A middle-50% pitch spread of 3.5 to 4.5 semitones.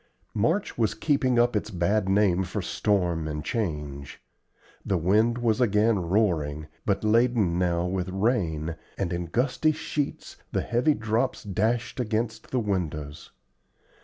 No: average, 5.1 semitones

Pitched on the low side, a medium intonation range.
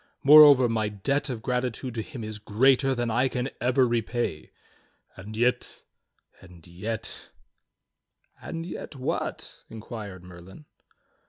Yes: low, 120 Hz; average, 3.7 semitones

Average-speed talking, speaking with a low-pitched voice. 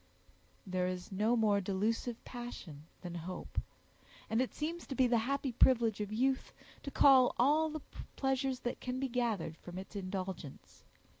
No: average, 160 wpm; high, 230 Hz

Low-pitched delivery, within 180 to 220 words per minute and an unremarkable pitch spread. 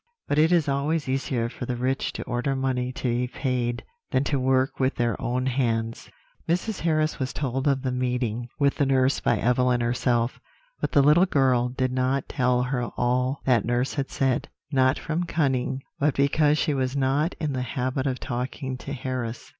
No: low, 130 Hz; average, 190 wpm; narrow, 2.0 semitones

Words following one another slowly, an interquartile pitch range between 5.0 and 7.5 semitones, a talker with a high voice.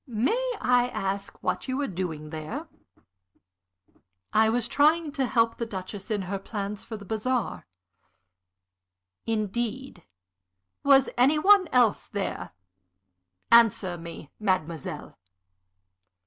Yes: slow, 110 wpm; average, 5.3 semitones; high, 225 Hz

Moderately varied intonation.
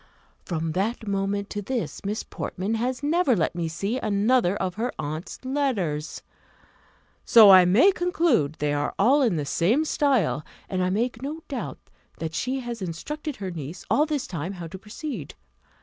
No: wide, 6.8 semitones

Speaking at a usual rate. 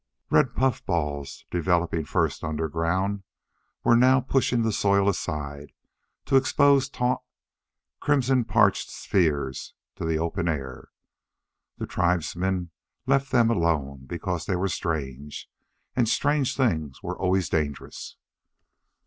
No: slow, 115 wpm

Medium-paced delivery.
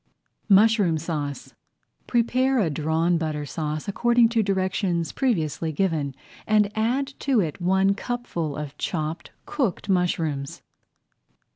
No: slow, 125 wpm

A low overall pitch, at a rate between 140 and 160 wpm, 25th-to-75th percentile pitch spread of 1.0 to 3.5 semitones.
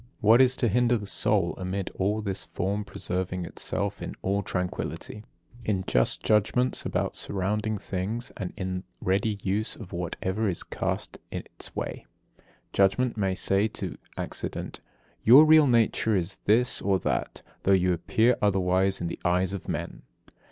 Yes: low, 100 Hz; average, 155 wpm; average, 2.9 semitones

